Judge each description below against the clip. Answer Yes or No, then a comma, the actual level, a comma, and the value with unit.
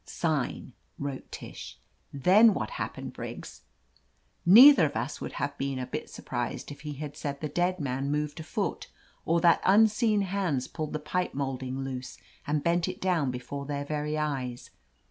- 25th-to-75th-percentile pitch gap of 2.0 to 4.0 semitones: No, average, 4.5 semitones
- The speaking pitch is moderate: Yes, medium, 150 Hz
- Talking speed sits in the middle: Yes, average, 170 wpm